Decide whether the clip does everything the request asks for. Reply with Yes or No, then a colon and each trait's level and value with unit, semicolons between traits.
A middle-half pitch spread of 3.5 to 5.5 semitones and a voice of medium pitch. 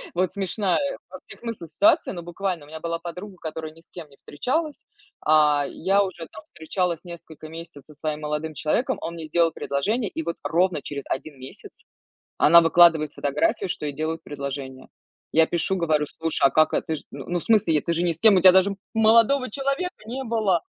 Yes: average, 3.9 semitones; medium, 170 Hz